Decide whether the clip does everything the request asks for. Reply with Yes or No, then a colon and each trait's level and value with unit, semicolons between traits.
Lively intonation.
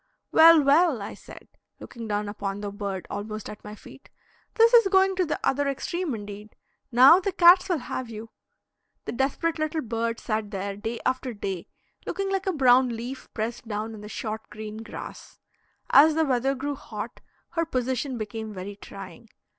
Yes: wide, 6.6 semitones